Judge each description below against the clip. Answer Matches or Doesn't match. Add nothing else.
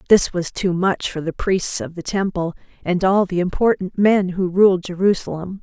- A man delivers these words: Doesn't match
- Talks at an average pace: Matches